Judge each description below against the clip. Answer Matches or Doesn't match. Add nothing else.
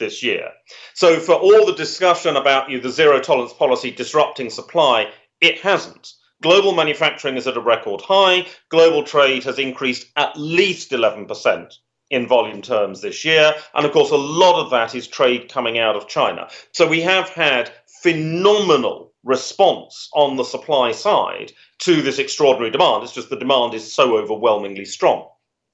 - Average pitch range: Doesn't match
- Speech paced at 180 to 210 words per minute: Doesn't match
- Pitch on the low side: Doesn't match